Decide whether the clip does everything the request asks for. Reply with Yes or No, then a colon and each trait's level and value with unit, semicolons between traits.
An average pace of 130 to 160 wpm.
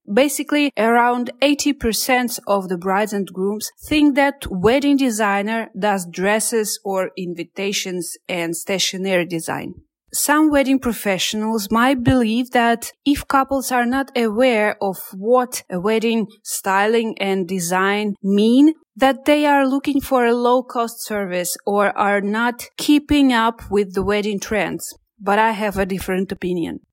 Yes: slow, 135 wpm